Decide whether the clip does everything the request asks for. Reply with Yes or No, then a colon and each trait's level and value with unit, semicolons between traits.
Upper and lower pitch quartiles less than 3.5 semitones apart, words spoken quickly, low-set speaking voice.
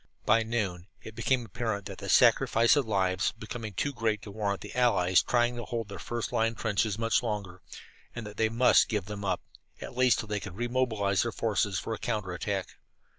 Yes: average, 2.8 semitones; fast, 215 wpm; low, 110 Hz